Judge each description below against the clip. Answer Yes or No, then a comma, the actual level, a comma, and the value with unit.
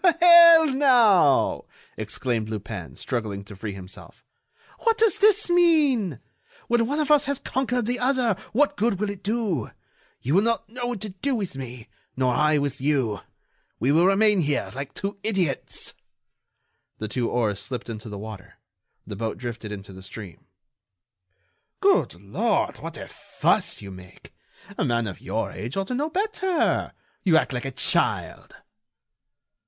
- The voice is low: No, medium, 170 Hz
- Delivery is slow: No, average, 160 wpm